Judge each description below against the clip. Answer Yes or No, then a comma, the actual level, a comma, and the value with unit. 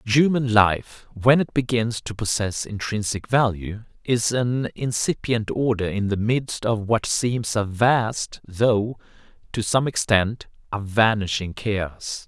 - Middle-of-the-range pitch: No, low, 110 Hz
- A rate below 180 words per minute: Yes, slow, 135 wpm